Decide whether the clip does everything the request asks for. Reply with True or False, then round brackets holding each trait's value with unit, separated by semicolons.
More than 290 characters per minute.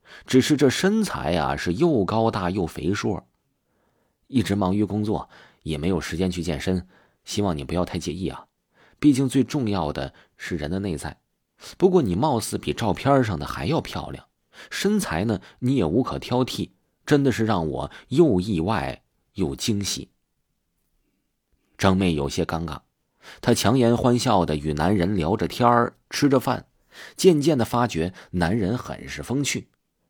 False (225 characters per minute)